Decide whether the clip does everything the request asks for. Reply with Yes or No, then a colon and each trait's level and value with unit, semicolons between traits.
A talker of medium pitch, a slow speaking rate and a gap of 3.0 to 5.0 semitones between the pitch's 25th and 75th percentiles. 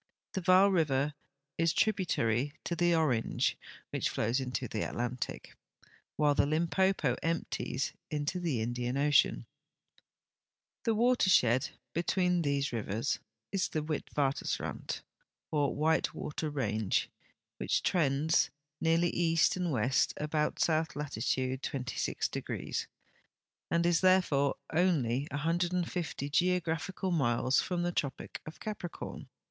Yes: medium, 150 Hz; slow, 115 wpm; average, 4.7 semitones